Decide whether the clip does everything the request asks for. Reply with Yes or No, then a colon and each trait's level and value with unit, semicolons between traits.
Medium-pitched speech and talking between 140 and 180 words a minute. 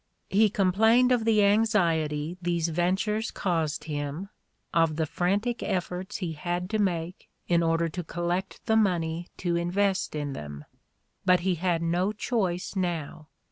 Yes: medium, 175 Hz; average, 145 wpm